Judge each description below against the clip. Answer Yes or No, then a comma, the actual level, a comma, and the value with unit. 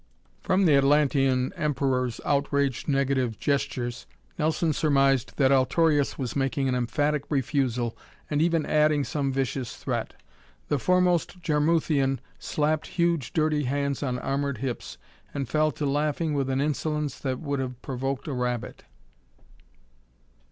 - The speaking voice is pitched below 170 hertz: Yes, medium, 140 Hz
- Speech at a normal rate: No, slow, 130 wpm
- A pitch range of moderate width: No, narrow, 2.3 semitones